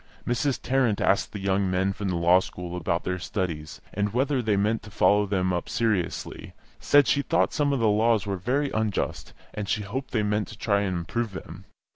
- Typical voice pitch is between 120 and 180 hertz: No, low, 105 Hz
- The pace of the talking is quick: Yes, fast, 210 wpm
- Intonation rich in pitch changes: No, average, 3.9 semitones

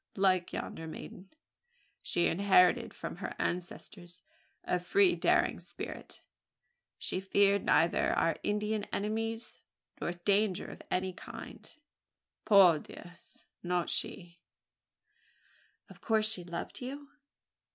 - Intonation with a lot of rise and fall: No, average, 3.2 semitones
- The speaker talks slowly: Yes, slow, 110 wpm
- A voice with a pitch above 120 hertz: Yes, high, 190 Hz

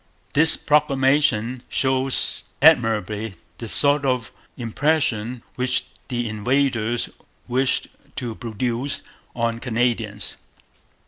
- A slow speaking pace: Yes, slow, 85 wpm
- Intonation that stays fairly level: No, average, 3.0 semitones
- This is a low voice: Yes, low, 125 Hz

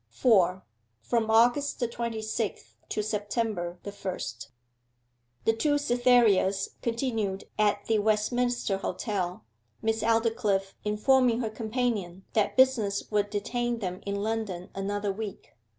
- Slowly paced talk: Yes, slow, 120 wpm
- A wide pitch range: No, average, 2.9 semitones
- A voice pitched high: Yes, high, 215 Hz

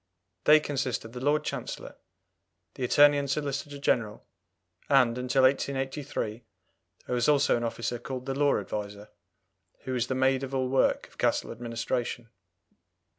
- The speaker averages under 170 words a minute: Yes, average, 150 wpm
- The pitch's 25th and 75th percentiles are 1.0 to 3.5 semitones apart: Yes, average, 2.7 semitones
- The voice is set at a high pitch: No, low, 130 Hz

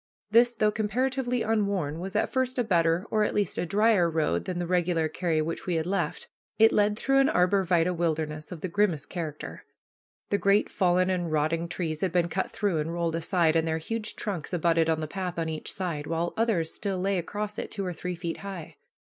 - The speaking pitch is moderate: Yes, medium, 180 Hz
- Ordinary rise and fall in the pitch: Yes, average, 3.9 semitones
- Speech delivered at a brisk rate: Yes, fast, 215 wpm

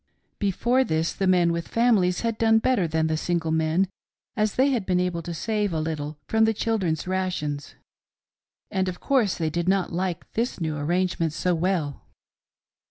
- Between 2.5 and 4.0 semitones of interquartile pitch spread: No, average, 4.6 semitones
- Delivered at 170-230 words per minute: Yes, average, 175 wpm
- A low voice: No, medium, 180 Hz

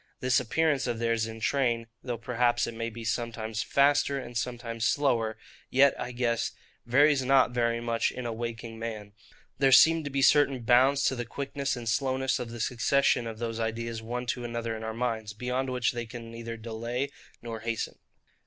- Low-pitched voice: Yes, low, 120 Hz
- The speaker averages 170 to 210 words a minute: Yes, average, 190 wpm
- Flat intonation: Yes, narrow, 2.3 semitones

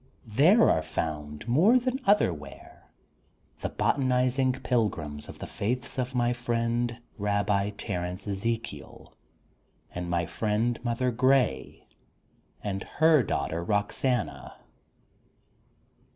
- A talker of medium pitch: No, low, 115 Hz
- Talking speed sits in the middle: No, slow, 105 wpm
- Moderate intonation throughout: No, wide, 5.8 semitones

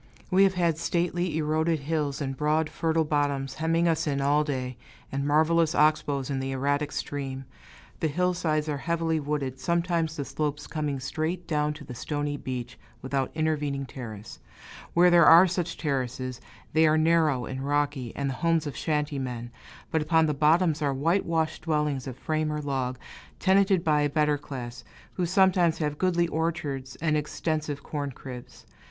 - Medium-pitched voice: Yes, medium, 150 Hz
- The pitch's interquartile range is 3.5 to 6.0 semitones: No, average, 2.9 semitones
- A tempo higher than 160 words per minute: Yes, average, 170 wpm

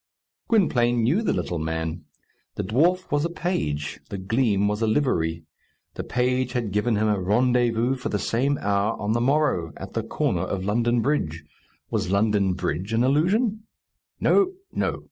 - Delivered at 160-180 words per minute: Yes, average, 165 wpm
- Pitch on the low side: Yes, low, 115 Hz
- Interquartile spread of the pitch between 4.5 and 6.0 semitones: Yes, wide, 5.4 semitones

